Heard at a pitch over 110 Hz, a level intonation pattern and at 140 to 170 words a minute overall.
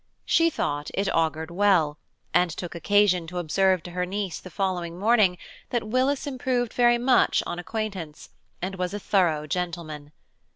No: medium, 185 Hz; average, 4.1 semitones; average, 160 wpm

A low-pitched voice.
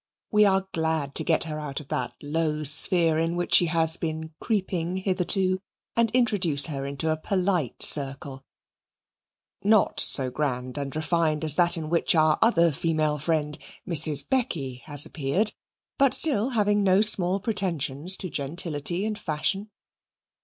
No: medium, 165 Hz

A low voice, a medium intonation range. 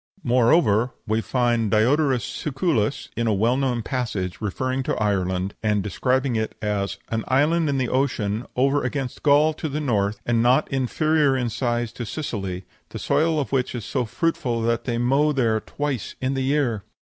Yes: low, 125 Hz; average, 3.9 semitones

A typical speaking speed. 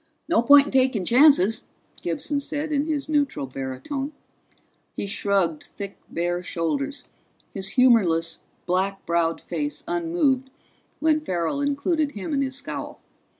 No: slow, 130 wpm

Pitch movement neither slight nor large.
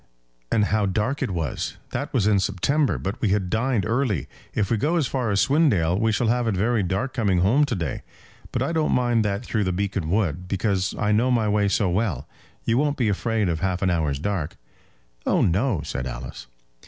Yes: average, 4.4 semitones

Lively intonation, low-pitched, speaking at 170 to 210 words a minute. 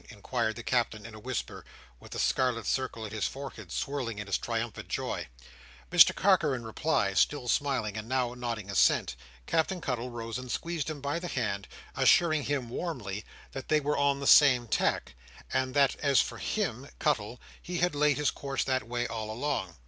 No: average, 4.2 semitones; low, 130 Hz; average, 185 wpm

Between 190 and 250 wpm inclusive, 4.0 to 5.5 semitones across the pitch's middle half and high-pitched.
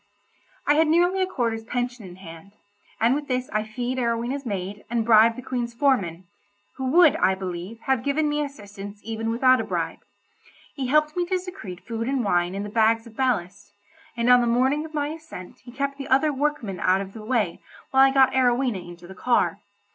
Yes: average, 200 wpm; average, 4.9 semitones; high, 240 Hz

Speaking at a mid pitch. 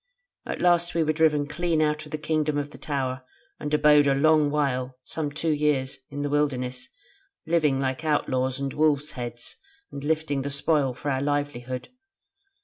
Yes: medium, 145 Hz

